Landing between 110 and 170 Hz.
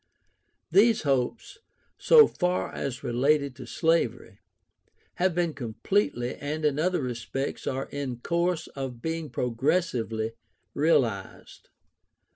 Yes: medium, 140 Hz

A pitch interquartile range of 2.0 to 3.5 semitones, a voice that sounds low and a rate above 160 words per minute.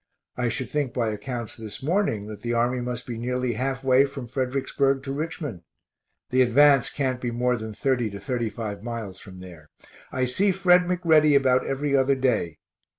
Yes: average, 3.1 semitones; low, 125 Hz; average, 180 wpm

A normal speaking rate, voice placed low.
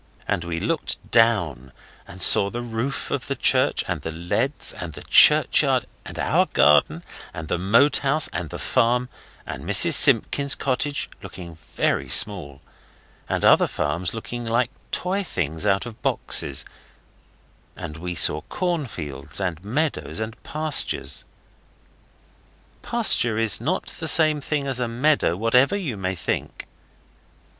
Yes: average, 145 wpm; low, 115 Hz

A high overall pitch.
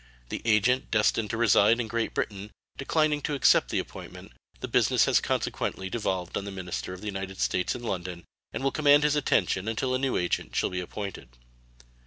No: low, 105 Hz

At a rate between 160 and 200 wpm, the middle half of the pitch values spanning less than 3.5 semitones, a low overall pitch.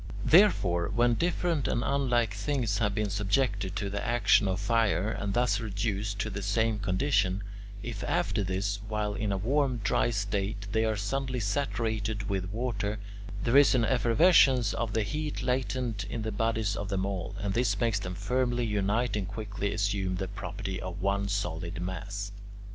Yes: average, 175 wpm; average, 3.1 semitones; low, 105 Hz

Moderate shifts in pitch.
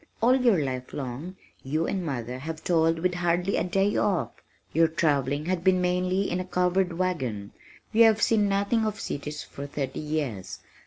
Yes: average, 4.7 semitones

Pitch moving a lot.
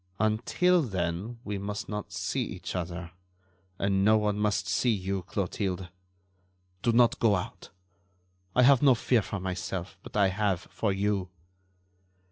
No: average, 2.8 semitones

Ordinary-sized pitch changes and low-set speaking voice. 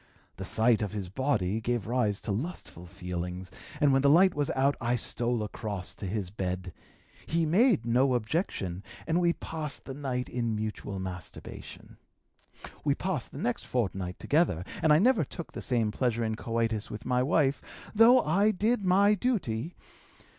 No: wide, 7.1 semitones; low, 120 Hz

